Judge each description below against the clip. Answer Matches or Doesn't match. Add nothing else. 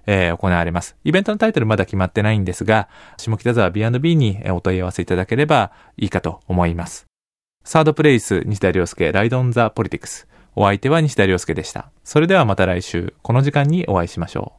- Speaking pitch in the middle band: Doesn't match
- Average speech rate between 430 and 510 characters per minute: Matches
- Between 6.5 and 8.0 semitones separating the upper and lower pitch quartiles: Doesn't match